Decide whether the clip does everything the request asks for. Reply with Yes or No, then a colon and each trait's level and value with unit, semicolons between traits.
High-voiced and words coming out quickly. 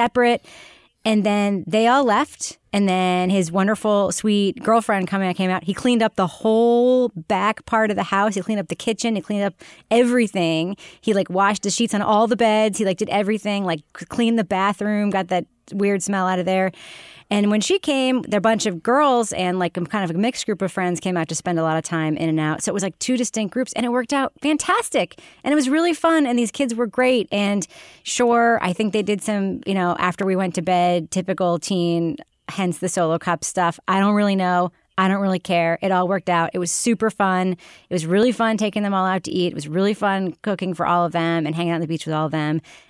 Yes: high, 200 Hz; fast, 245 wpm